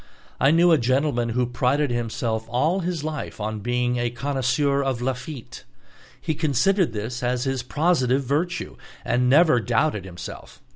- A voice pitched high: No, low, 130 Hz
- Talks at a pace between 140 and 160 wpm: Yes, average, 150 wpm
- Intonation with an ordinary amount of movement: Yes, average, 3.9 semitones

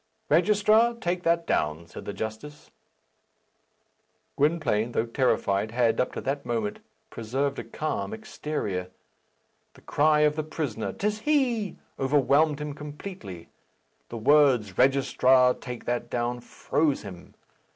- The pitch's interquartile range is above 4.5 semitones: Yes, average, 5.3 semitones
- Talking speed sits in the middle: No, slow, 125 wpm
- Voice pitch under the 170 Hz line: Yes, medium, 140 Hz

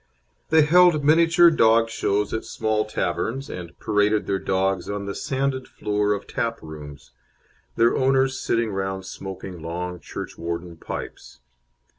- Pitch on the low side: Yes, low, 105 Hz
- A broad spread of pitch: Yes, wide, 5.9 semitones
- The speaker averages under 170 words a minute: Yes, average, 140 wpm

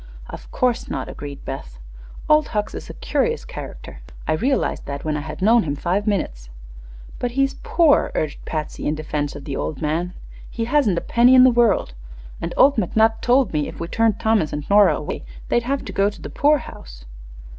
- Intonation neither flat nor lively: No, wide, 8.4 semitones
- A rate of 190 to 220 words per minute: Yes, average, 195 wpm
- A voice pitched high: Yes, high, 205 Hz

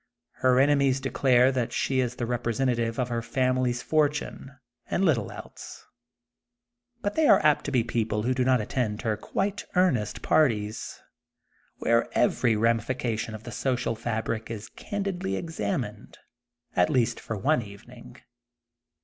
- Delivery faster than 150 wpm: No, average, 145 wpm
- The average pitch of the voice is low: Yes, low, 125 Hz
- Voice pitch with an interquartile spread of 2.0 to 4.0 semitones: Yes, average, 3.1 semitones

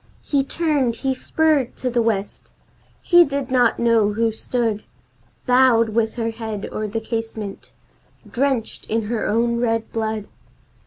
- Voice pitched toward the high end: Yes, high, 230 Hz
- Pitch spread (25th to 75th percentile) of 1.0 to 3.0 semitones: Yes, narrow, 2.5 semitones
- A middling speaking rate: Yes, average, 145 wpm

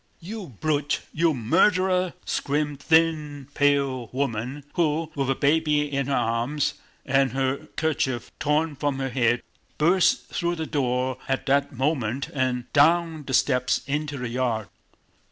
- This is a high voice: No, medium, 140 Hz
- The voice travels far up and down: No, average, 3.2 semitones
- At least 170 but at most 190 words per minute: No, average, 145 wpm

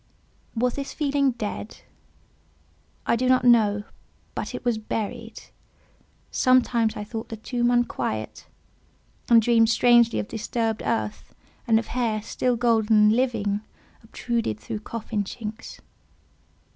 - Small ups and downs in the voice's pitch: Yes, narrow, 2.1 semitones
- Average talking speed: No, slow, 125 wpm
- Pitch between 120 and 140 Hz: No, high, 230 Hz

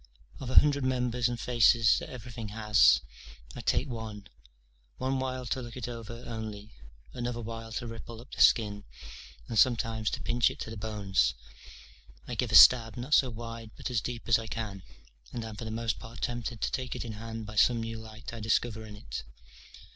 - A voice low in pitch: Yes, low, 115 Hz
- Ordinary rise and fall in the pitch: No, narrow, 1.8 semitones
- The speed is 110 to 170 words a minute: No, average, 200 wpm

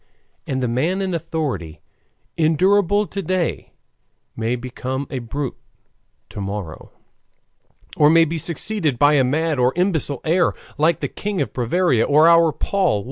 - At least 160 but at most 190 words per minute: No, average, 150 wpm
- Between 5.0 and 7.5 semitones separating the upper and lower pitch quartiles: Yes, wide, 5.4 semitones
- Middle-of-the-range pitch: Yes, medium, 155 Hz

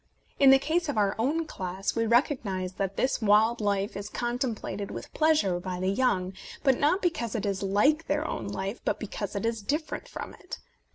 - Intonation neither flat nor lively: No, wide, 6.2 semitones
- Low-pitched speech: No, high, 220 Hz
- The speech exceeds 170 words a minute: Yes, average, 195 wpm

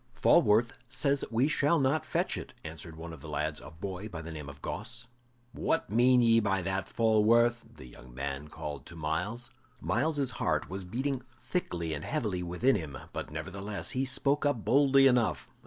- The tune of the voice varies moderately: No, wide, 7.8 semitones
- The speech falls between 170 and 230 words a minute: Yes, average, 180 wpm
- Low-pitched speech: Yes, low, 105 Hz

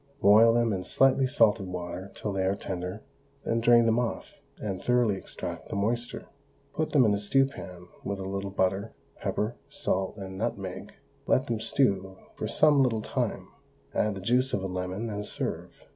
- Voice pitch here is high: No, low, 105 Hz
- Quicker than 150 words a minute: Yes, average, 180 wpm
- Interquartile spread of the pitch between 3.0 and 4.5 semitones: Yes, average, 3.7 semitones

